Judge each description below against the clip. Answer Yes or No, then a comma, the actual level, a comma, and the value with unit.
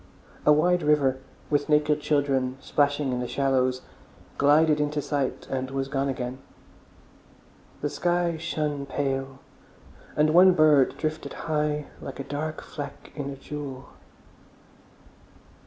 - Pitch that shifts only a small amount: Yes, narrow, 2.1 semitones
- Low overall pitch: No, medium, 145 Hz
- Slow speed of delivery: Yes, slow, 125 wpm